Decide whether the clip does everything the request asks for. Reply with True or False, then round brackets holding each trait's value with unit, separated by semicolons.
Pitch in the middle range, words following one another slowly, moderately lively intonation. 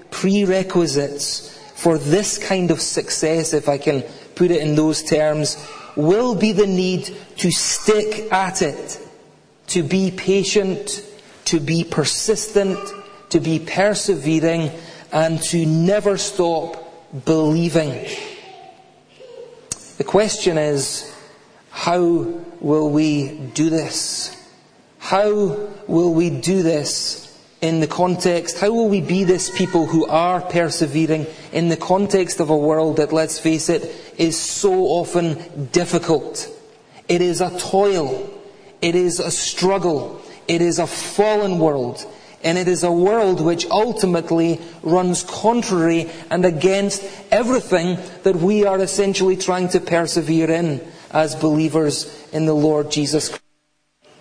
True (175 Hz; 125 wpm; 3.6 semitones)